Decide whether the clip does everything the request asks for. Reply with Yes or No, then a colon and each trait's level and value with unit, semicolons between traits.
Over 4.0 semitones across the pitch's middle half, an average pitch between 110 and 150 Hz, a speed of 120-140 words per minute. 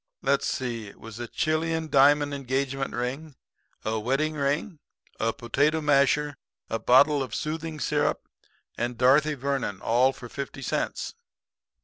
No: average, 3.2 semitones; medium, 140 Hz; slow, 135 wpm